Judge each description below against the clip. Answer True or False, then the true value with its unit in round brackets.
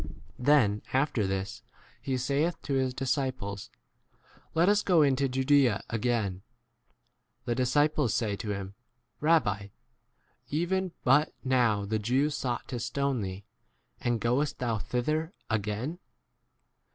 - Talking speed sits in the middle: False (130 wpm)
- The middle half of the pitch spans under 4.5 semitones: False (5.1 semitones)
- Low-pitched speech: True (125 Hz)